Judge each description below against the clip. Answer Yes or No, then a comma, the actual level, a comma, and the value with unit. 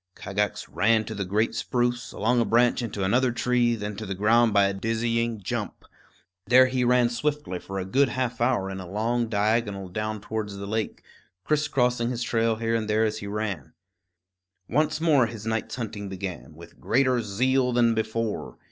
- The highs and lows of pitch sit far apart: No, average, 2.9 semitones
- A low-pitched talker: Yes, low, 115 Hz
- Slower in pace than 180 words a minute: No, average, 185 wpm